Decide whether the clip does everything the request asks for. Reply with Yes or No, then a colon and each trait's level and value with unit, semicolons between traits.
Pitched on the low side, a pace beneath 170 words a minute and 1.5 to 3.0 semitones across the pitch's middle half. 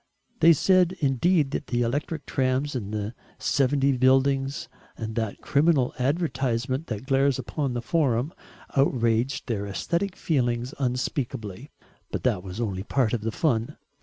No: low, 130 Hz; average, 140 wpm; average, 3.5 semitones